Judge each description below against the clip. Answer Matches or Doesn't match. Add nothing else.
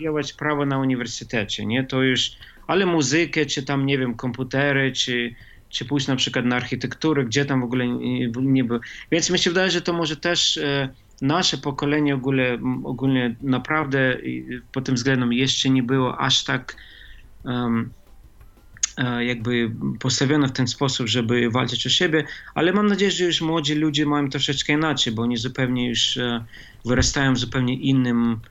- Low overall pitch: Matches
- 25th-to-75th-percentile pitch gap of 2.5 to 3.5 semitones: Matches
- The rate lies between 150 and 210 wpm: Matches